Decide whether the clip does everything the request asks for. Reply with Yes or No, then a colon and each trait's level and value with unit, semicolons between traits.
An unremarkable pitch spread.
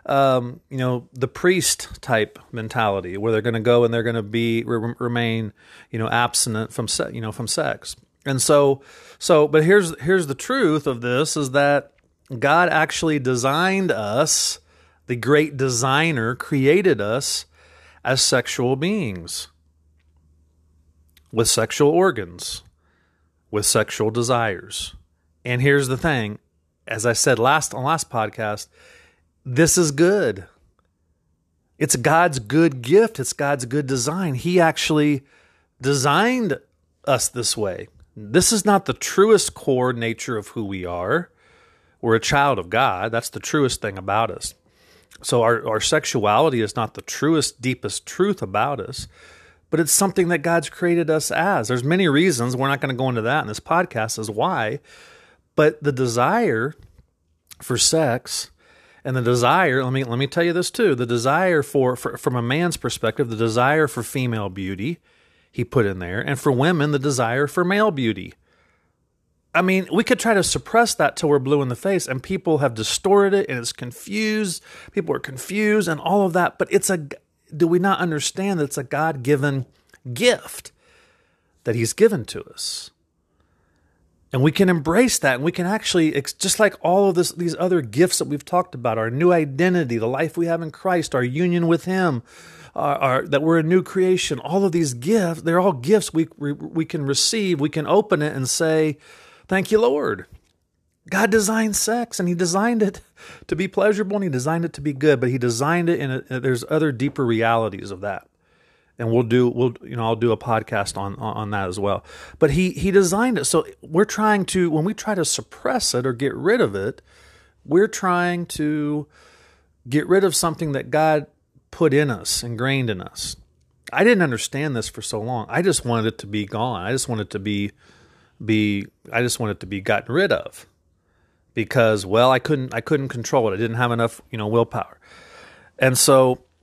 No: wide, 7.0 semitones